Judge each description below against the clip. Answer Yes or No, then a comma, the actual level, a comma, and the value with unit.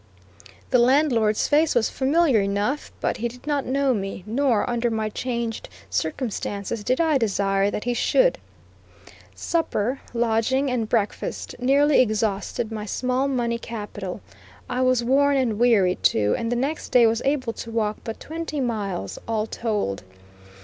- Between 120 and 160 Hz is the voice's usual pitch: No, high, 235 Hz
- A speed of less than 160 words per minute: Yes, average, 150 wpm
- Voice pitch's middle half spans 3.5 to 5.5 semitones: Yes, average, 3.8 semitones